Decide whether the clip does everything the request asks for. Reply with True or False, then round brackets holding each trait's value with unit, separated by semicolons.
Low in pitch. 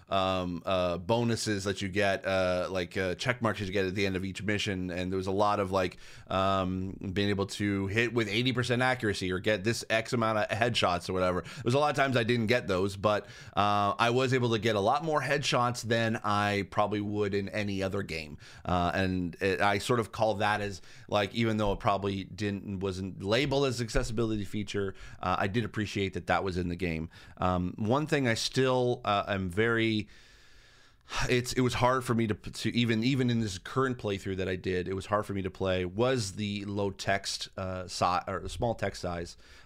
True (105 Hz)